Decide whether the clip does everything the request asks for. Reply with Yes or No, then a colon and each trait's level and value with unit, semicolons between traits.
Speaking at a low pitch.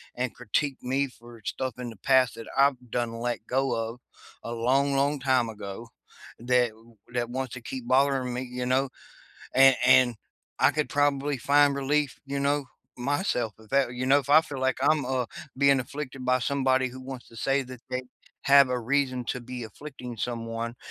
Yes: low, 130 Hz